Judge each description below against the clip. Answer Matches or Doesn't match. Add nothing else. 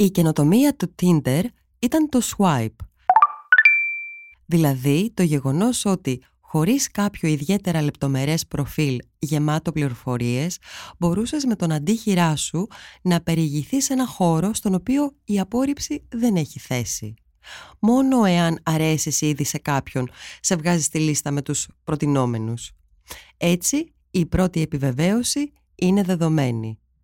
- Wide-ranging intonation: Matches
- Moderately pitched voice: Matches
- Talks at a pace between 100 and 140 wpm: Matches